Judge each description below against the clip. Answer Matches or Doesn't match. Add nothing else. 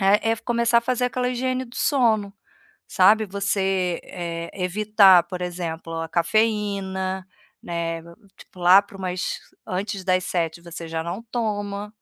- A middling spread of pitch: Matches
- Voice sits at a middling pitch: Doesn't match